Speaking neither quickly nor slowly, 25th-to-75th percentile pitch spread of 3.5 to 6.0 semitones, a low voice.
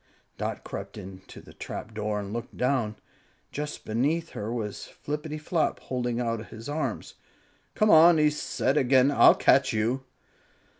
Yes: average, 145 wpm; average, 5.2 semitones; low, 125 Hz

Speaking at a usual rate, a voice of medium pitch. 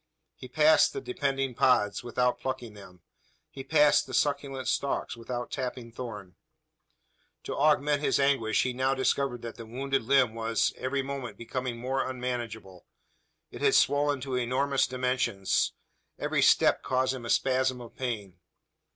No: average, 150 wpm; low, 130 Hz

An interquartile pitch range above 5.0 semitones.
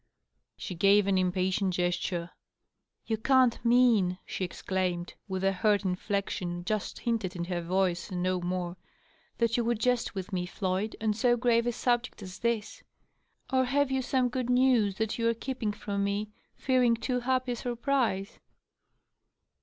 No: average, 4.6 semitones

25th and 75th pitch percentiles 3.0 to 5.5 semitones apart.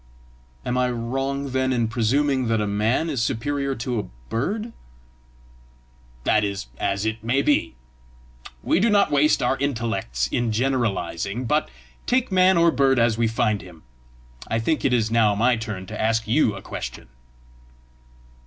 Yes: average, 4.1 semitones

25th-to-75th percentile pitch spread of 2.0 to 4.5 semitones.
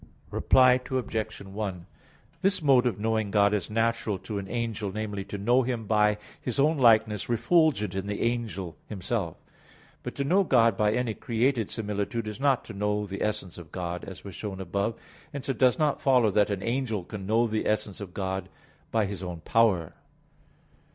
Yes: average, 3.2 semitones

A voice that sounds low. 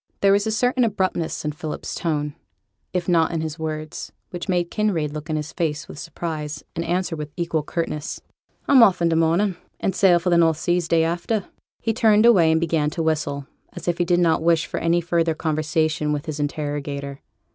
No: medium, 165 Hz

